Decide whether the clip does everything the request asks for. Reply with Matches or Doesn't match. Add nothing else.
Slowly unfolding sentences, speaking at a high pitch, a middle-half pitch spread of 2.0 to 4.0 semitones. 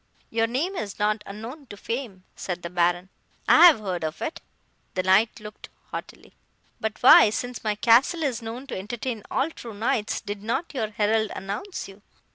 Doesn't match